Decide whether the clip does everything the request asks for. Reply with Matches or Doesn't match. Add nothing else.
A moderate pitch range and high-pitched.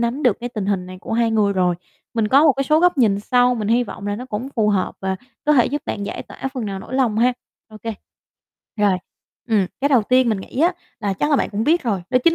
Matches